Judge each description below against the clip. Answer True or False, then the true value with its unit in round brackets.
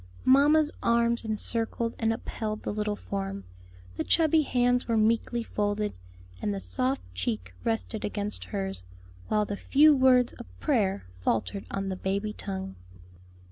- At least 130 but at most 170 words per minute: True (140 wpm)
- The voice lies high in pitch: True (210 Hz)